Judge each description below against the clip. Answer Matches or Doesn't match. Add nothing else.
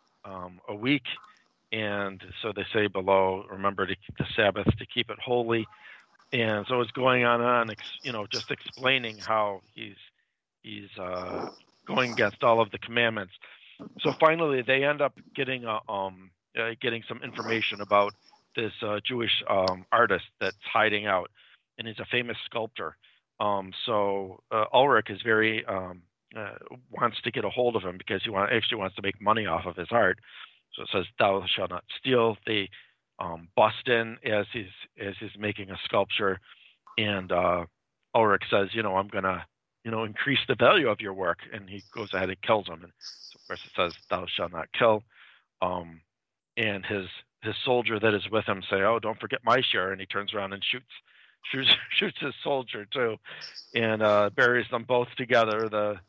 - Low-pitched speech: Matches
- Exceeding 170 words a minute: Matches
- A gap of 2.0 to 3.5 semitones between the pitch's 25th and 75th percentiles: Matches